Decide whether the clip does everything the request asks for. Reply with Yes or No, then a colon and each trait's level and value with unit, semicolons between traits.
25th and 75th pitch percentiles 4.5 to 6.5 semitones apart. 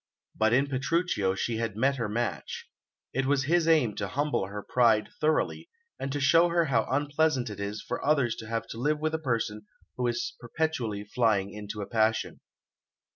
Yes: average, 5.1 semitones